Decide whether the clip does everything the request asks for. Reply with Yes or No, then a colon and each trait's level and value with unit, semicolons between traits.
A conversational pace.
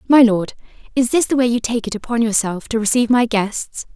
No: fast, 230 wpm